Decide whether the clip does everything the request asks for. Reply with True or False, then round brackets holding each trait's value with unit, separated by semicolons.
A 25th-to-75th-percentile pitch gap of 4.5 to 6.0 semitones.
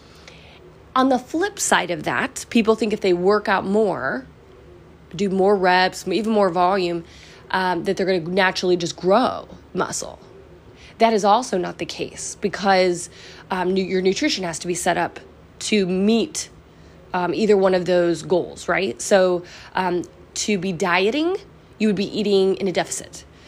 False (2.5 semitones)